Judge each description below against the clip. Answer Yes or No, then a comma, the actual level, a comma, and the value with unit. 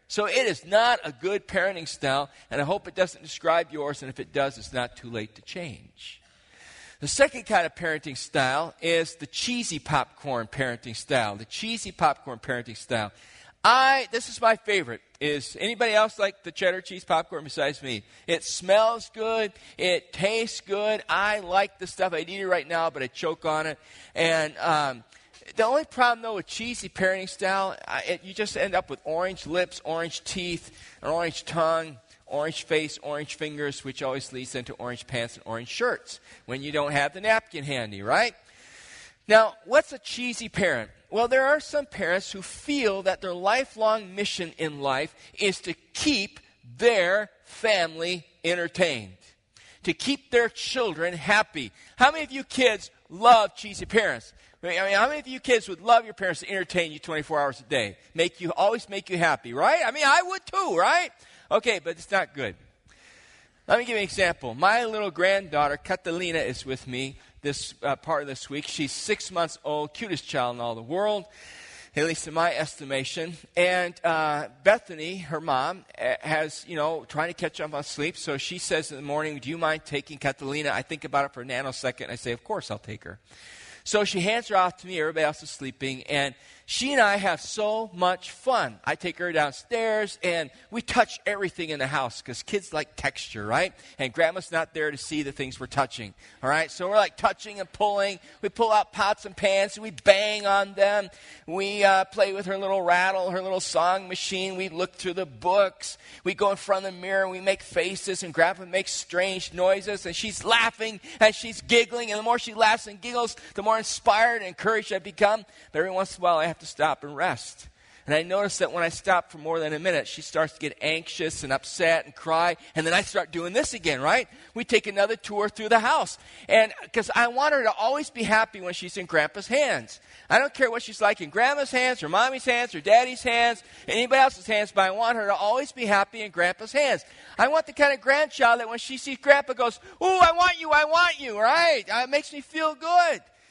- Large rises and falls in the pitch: Yes, wide, 6.3 semitones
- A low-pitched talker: No, medium, 185 Hz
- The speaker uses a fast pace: Yes, fast, 210 wpm